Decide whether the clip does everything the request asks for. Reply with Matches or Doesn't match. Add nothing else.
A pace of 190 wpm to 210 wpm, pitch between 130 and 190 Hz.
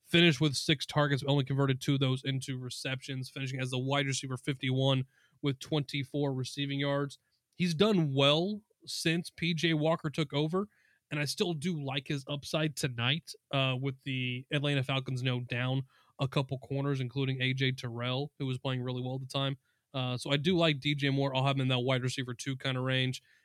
Matches